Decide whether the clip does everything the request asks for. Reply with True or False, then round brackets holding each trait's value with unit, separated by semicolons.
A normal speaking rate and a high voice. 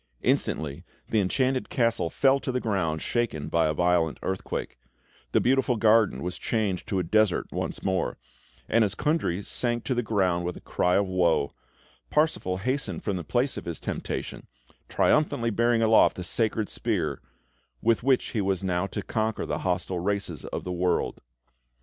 False (170 wpm; 100 Hz)